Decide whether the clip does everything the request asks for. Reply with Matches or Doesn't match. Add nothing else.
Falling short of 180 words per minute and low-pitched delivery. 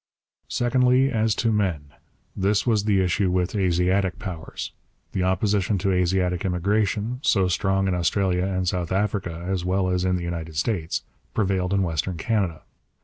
Matches